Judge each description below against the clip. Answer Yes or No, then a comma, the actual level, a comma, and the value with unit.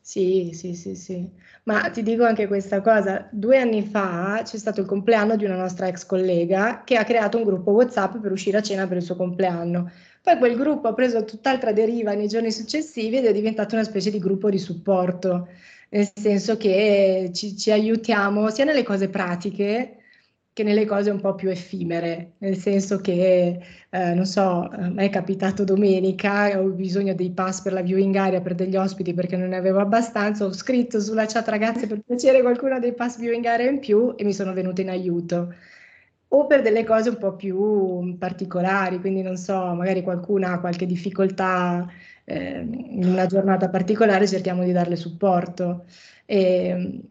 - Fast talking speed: Yes, fast, 180 wpm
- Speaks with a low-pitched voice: No, high, 195 Hz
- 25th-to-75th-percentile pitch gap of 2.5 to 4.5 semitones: Yes, average, 3.0 semitones